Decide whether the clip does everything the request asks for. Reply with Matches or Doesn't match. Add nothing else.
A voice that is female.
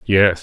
Doesn't match